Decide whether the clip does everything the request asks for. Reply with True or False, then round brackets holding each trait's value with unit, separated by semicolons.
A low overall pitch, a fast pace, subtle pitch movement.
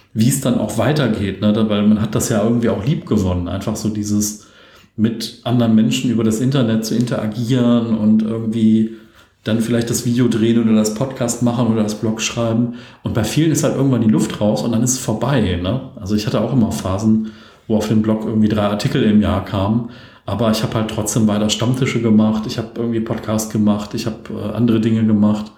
True (110 Hz; 210 wpm; 1.8 semitones)